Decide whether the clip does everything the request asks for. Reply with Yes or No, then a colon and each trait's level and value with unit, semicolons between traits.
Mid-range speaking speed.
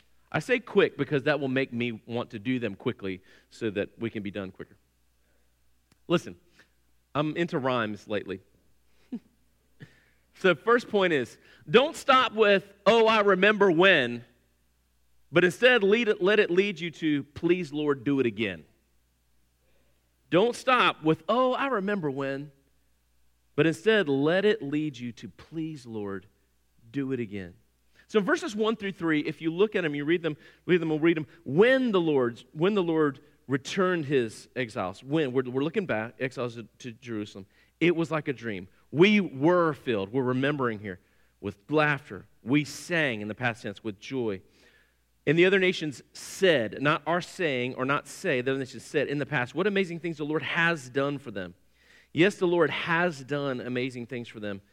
Yes: average, 180 wpm